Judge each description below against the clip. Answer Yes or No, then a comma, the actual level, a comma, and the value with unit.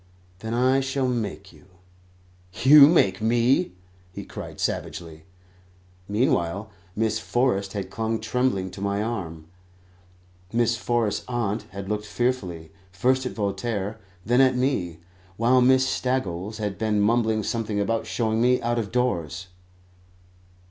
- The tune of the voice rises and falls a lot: No, average, 3.8 semitones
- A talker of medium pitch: No, low, 110 Hz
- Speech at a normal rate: No, slow, 130 wpm